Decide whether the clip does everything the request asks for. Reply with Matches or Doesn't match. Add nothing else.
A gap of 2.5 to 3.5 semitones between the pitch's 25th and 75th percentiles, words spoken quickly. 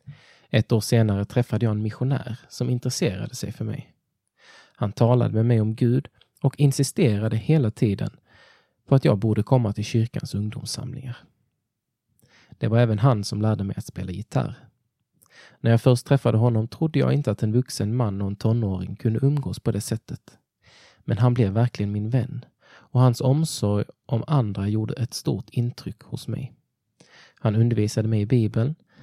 Doesn't match